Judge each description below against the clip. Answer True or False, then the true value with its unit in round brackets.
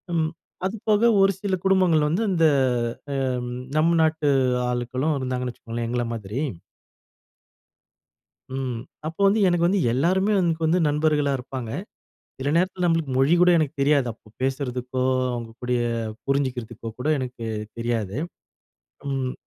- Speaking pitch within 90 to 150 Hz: True (140 Hz)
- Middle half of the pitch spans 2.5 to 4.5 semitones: False (5.4 semitones)